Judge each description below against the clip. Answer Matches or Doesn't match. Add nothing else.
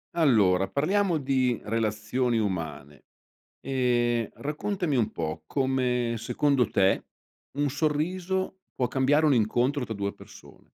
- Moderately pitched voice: Doesn't match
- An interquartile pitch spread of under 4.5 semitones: Doesn't match